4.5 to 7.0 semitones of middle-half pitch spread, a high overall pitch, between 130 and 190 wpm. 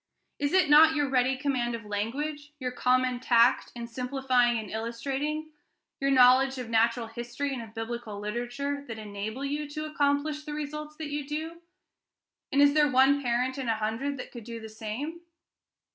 No: average, 3.7 semitones; very high, 260 Hz; average, 175 wpm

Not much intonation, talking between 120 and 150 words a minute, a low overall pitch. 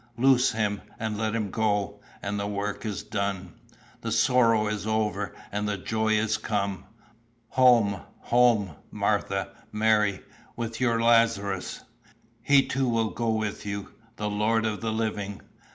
Yes: narrow, 1.9 semitones; average, 145 wpm; low, 110 Hz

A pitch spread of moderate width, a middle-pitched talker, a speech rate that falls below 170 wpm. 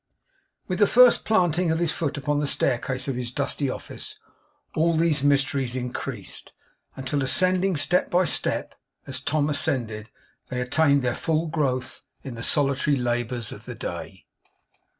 Yes: average, 4.2 semitones; medium, 145 Hz; average, 150 wpm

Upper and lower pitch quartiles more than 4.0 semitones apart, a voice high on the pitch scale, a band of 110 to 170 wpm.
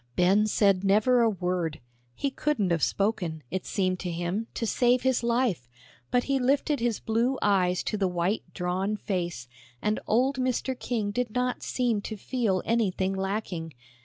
Yes: average, 4.9 semitones; high, 210 Hz; average, 165 wpm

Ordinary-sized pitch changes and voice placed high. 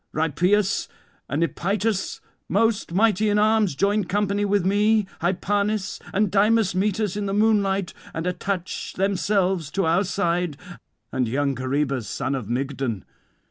Yes: average, 4.2 semitones; high, 195 Hz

